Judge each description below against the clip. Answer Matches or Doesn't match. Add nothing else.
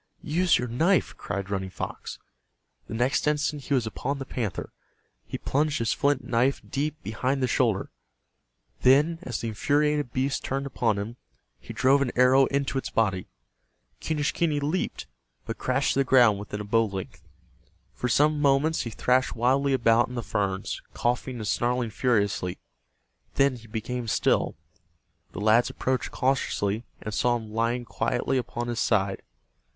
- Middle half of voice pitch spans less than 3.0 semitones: Doesn't match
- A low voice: Matches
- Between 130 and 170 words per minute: Matches